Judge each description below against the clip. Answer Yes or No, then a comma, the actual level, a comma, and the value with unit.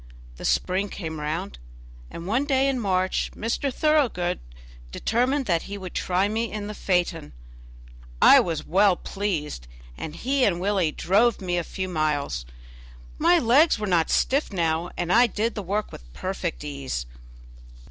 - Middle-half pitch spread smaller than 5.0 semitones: No, wide, 5.5 semitones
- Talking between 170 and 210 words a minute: No, average, 155 wpm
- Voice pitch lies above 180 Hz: Yes, high, 190 Hz